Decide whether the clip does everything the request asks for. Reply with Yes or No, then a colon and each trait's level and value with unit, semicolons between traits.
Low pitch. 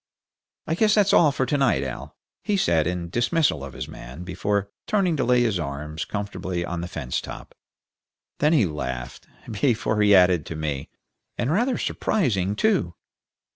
Yes: low, 100 Hz